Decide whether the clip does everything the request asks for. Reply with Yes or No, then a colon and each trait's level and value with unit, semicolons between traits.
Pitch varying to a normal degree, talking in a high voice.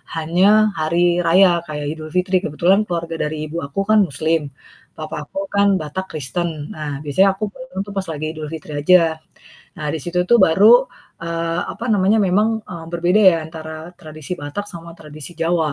No: average, 3.2 semitones; medium, 165 Hz